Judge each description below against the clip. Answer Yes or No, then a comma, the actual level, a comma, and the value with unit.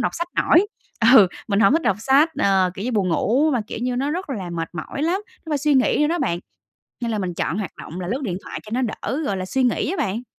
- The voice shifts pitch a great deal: Yes, wide, 7.1 semitones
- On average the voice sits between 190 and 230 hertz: No, high, 240 Hz